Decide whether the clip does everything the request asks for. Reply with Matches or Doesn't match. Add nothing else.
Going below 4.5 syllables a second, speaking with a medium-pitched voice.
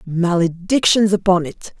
Matches